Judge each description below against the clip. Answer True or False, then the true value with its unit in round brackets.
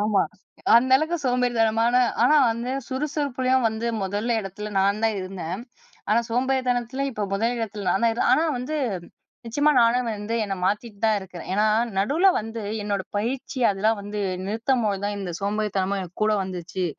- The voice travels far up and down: False (3.6 semitones)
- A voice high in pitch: True (220 Hz)